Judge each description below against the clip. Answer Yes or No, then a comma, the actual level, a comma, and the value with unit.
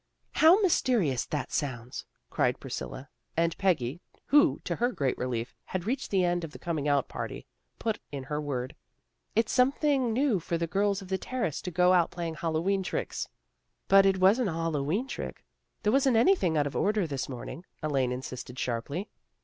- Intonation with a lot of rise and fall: Yes, wide, 6.9 semitones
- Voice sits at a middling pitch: Yes, medium, 170 Hz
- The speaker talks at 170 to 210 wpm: Yes, average, 190 wpm